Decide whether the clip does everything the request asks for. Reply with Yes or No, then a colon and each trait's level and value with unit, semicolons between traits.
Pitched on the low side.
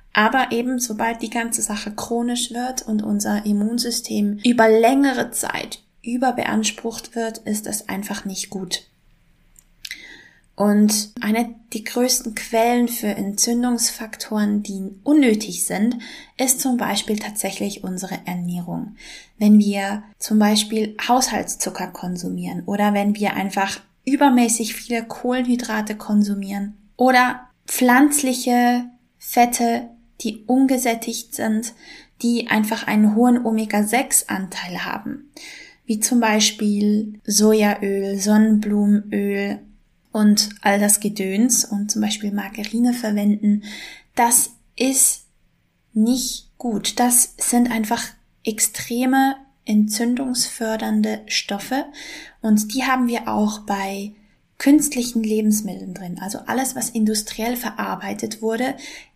No: high, 225 Hz